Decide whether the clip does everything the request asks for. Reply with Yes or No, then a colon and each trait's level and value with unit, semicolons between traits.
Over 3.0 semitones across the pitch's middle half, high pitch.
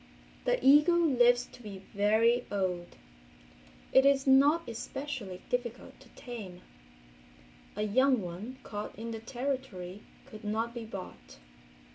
Yes: average, 4.5 semitones; high, 235 Hz